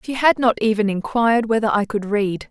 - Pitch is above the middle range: Yes, high, 220 Hz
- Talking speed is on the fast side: Yes, fast, 215 wpm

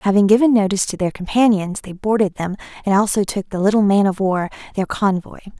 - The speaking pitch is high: Yes, high, 200 Hz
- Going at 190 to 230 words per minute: Yes, fast, 205 wpm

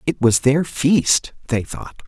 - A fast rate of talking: No, average, 175 wpm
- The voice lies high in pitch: No, medium, 140 Hz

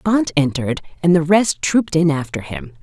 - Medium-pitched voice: Yes, medium, 160 Hz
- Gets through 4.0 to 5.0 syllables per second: No, 5.4 syllables/s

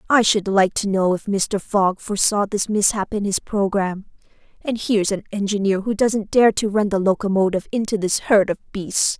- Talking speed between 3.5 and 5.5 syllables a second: Yes, 5.1 syllables/s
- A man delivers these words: No, female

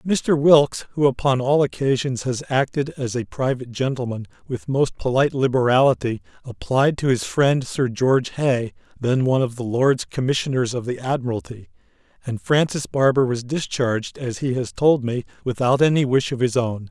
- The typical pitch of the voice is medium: No, low, 130 Hz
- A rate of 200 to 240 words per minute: No, average, 170 wpm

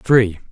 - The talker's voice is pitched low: Yes, low, 110 Hz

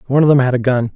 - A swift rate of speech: Yes, fast, 380 wpm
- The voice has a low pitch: Yes, low, 130 Hz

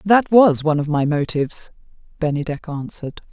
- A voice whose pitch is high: No, medium, 160 Hz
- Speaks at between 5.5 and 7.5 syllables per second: Yes, 5.8 syllables/s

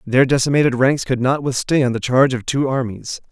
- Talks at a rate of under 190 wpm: No, average, 200 wpm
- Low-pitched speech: Yes, low, 130 Hz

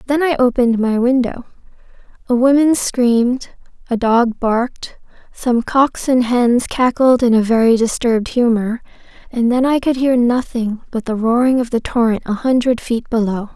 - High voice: Yes, high, 240 Hz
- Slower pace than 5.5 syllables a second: Yes, 4.7 syllables/s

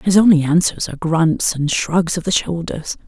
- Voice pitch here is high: No, medium, 170 Hz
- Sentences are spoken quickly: No, average, 195 wpm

